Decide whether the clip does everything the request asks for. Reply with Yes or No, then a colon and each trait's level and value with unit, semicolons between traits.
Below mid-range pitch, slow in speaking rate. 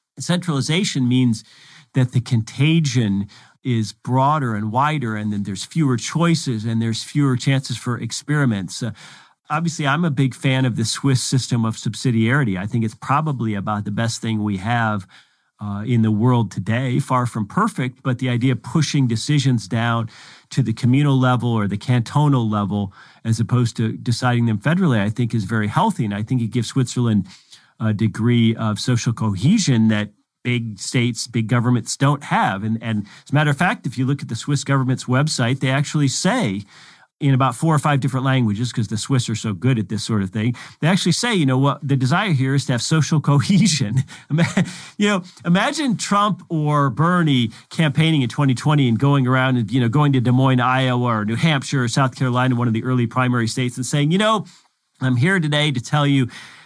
No: low, 130 Hz; average, 195 wpm